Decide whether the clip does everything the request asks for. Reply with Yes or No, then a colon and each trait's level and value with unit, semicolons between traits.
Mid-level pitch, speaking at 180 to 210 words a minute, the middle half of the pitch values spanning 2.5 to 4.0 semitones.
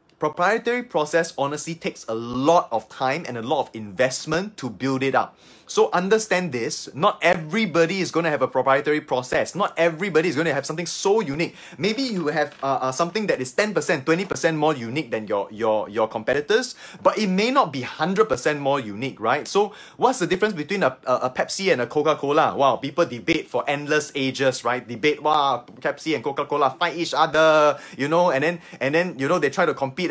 No: medium, 160 Hz; fast, 205 wpm; average, 5.1 semitones